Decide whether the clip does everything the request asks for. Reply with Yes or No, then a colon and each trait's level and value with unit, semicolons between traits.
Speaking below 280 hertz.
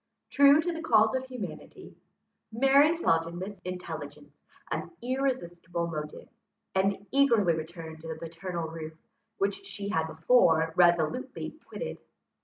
Yes: high, 190 Hz